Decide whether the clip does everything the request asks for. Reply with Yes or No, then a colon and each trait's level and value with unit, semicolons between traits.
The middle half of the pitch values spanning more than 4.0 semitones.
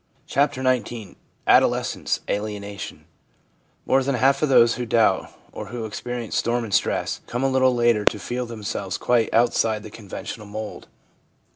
No: average, 2.8 semitones